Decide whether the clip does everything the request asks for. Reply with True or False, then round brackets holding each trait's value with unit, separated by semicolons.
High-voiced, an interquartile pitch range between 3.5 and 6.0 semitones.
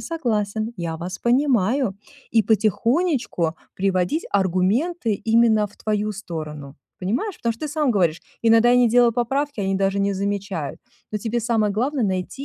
True (215 Hz; 4.0 semitones)